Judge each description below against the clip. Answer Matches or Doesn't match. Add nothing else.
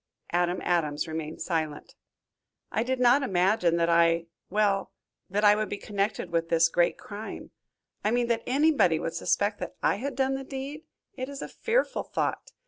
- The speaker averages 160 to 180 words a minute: Matches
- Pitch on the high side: Matches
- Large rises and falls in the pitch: Matches